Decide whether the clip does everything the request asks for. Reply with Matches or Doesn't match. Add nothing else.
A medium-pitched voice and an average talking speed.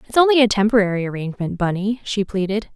Doesn't match